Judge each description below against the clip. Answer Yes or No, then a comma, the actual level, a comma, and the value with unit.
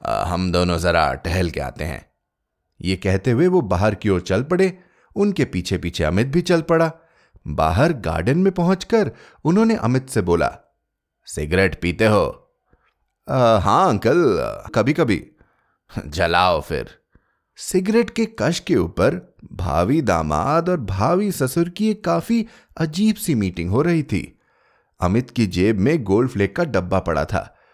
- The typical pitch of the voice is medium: No, low, 125 Hz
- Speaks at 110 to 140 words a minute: No, average, 150 wpm